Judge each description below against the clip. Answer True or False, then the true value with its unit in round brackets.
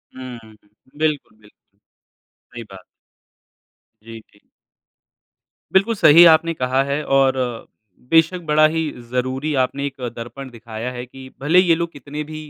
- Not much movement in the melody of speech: False (4.3 semitones)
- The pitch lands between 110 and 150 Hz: True (135 Hz)